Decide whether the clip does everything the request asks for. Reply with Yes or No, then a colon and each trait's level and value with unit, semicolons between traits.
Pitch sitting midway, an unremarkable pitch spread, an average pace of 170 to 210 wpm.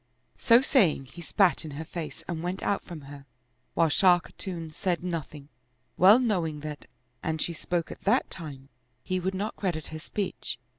Yes: medium, 170 Hz; average, 3.4 semitones; average, 180 wpm